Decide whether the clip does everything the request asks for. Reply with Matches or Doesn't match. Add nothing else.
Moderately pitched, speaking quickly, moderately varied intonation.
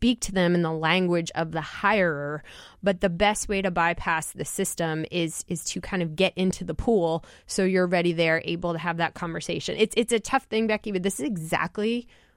Matches